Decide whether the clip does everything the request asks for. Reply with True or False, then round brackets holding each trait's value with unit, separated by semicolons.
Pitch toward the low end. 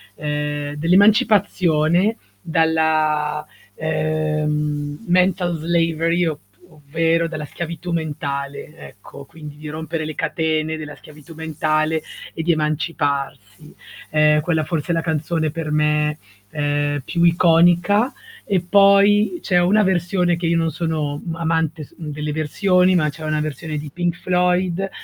False (160 Hz)